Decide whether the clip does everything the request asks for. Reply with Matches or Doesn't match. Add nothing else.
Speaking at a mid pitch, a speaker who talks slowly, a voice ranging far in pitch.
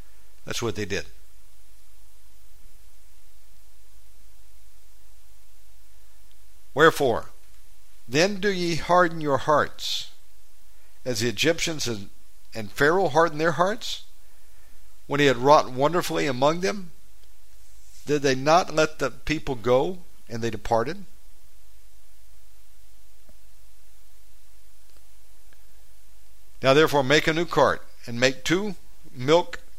Doesn't match